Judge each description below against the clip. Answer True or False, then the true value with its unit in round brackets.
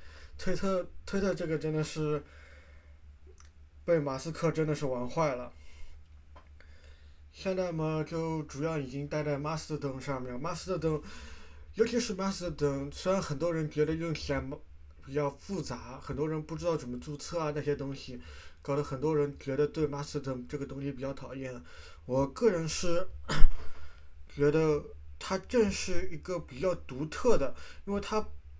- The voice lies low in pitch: False (145 Hz)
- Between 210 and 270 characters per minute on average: True (230 characters per minute)